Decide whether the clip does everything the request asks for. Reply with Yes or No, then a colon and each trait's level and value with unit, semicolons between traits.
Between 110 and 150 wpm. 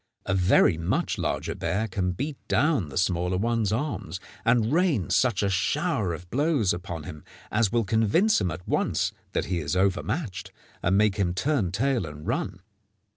No: average, 175 wpm